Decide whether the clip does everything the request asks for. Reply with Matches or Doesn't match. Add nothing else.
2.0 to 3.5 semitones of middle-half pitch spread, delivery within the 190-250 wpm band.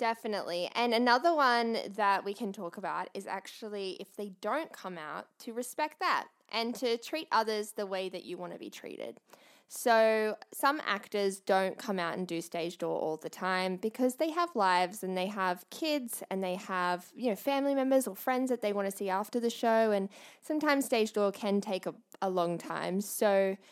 Doesn't match